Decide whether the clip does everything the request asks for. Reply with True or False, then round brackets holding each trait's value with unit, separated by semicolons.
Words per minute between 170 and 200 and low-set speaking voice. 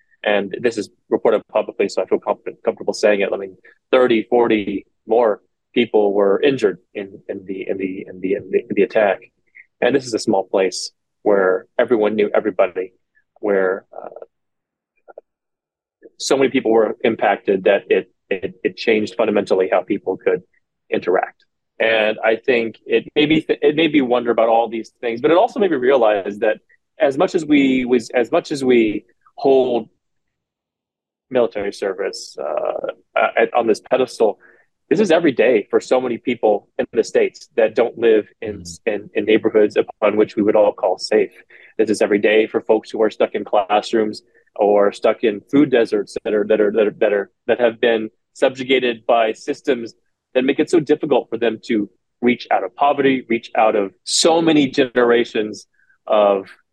True (180 wpm; 130 Hz)